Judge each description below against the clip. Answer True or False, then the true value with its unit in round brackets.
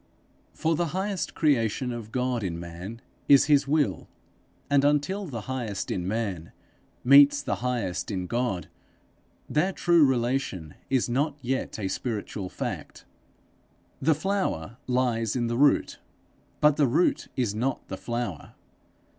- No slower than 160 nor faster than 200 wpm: False (140 wpm)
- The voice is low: True (125 Hz)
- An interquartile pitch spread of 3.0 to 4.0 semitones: False (4.9 semitones)